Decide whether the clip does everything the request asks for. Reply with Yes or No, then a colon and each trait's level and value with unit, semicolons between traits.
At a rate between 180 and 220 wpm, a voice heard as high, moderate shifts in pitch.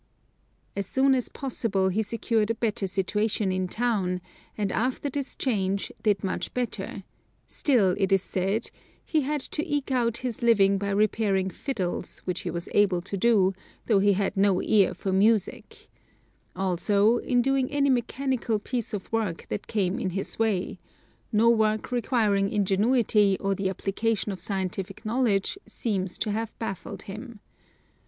No: average, 155 wpm; high, 210 Hz; average, 3.5 semitones